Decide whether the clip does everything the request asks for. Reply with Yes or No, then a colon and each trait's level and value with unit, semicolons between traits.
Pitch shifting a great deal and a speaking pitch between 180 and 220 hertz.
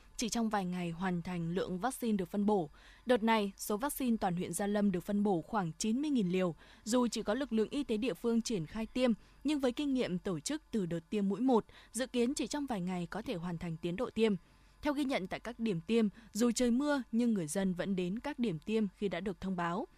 No: average, 4.6 semitones; high, 215 Hz